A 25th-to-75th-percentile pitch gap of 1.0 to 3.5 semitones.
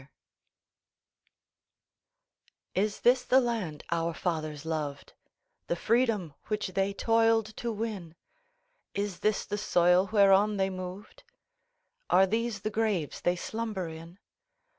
No: average, 4.2 semitones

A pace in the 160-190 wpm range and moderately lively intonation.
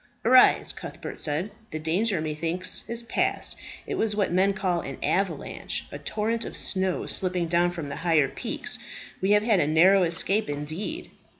Yes: average, 170 wpm; average, 4.2 semitones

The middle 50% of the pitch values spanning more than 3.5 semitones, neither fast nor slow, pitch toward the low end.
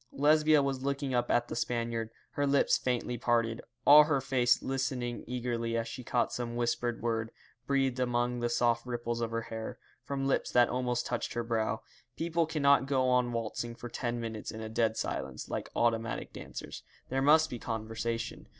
No: narrow, 2.5 semitones; average, 180 wpm; low, 120 Hz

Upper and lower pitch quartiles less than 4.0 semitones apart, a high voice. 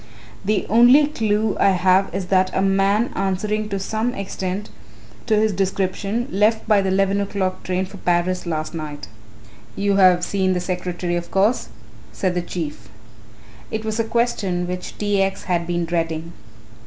Yes: average, 2.7 semitones; high, 195 Hz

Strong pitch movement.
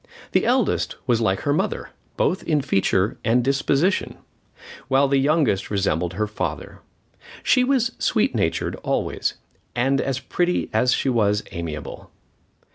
Yes: wide, 6.0 semitones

